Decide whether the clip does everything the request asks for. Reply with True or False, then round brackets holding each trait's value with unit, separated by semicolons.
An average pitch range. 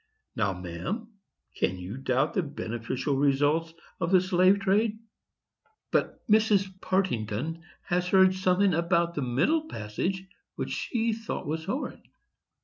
False (6.5 semitones)